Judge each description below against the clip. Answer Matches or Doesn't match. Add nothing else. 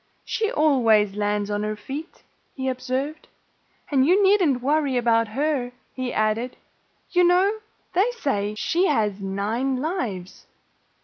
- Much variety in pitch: Matches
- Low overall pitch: Doesn't match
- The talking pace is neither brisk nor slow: Doesn't match